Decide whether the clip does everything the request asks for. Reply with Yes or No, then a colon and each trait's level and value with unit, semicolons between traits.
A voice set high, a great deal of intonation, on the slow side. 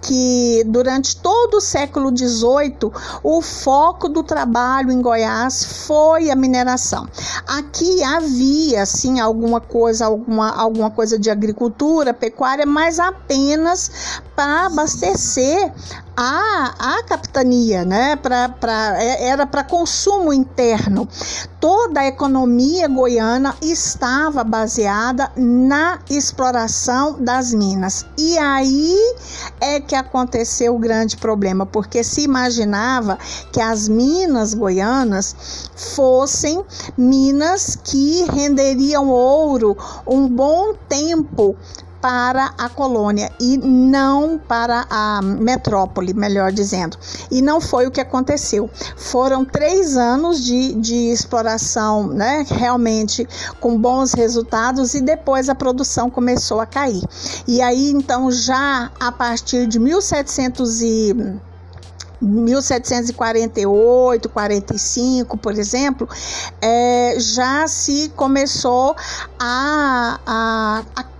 No: very high, 255 Hz; average, 3.6 semitones; slow, 105 wpm